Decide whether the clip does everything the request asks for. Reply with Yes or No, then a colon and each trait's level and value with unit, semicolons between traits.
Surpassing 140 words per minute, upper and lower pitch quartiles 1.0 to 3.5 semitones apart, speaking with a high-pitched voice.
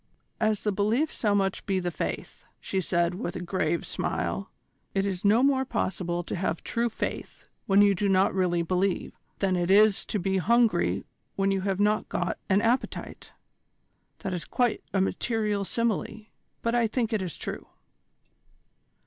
Yes: average, 170 wpm; average, 2.8 semitones; high, 195 Hz